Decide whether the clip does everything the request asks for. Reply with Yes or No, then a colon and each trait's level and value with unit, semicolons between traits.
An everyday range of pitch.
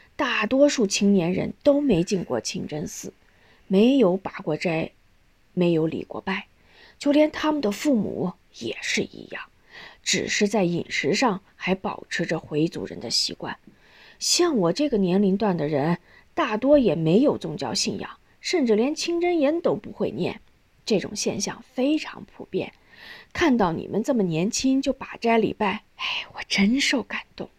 No: wide, 6.9 semitones